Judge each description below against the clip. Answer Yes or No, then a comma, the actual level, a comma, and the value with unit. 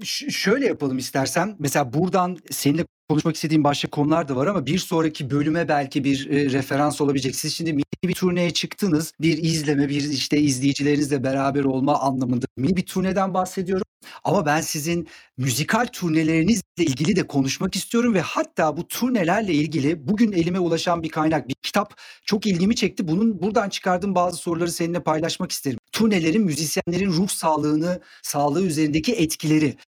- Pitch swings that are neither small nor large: Yes, average, 4.1 semitones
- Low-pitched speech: No, medium, 160 Hz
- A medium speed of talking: No, fast, 160 wpm